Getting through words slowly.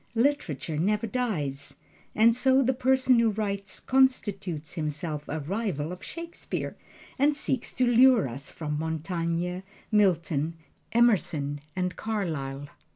Yes: slow, 120 wpm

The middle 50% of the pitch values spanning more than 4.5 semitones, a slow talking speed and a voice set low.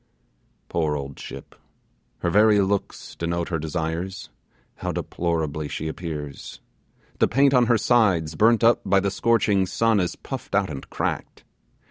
No: average, 5.2 semitones; average, 145 wpm; very low, 95 Hz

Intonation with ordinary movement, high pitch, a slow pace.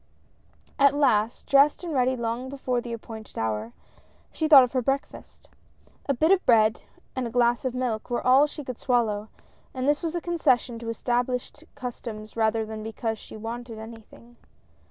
No: average, 3.2 semitones; high, 240 Hz; average, 175 wpm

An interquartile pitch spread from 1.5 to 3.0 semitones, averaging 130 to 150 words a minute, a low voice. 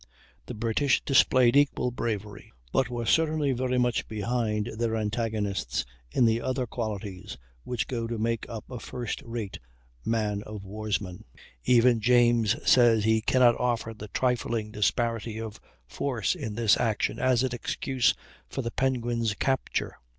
Yes: narrow, 2.5 semitones; average, 145 wpm; low, 115 Hz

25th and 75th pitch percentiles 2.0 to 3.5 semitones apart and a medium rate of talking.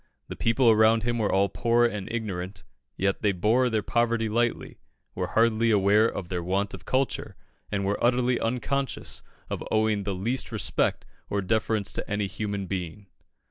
Yes: average, 2.9 semitones; average, 170 wpm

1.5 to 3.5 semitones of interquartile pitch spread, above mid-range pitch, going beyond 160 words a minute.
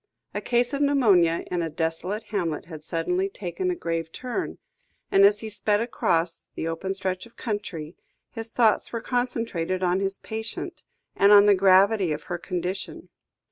No: average, 4.5 semitones; high, 195 Hz; average, 170 wpm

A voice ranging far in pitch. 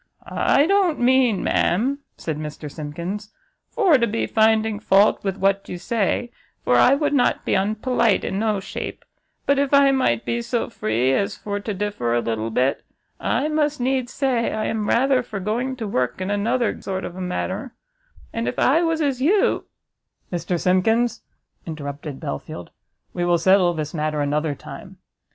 Yes: wide, 6.6 semitones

